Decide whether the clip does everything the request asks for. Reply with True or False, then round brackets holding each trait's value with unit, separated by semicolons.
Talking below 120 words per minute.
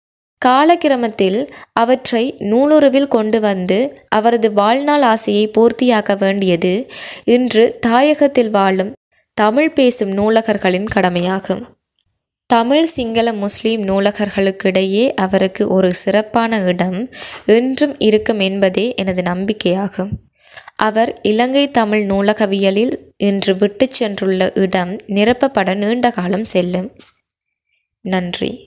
True (90 wpm)